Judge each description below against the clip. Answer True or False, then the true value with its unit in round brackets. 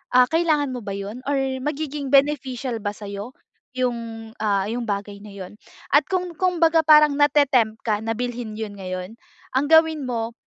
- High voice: True (250 Hz)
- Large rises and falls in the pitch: True (5.8 semitones)